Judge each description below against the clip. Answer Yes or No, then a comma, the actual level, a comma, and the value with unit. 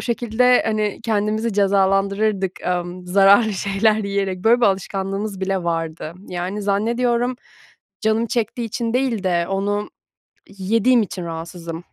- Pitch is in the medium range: No, high, 200 Hz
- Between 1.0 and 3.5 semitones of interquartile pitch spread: Yes, average, 2.8 semitones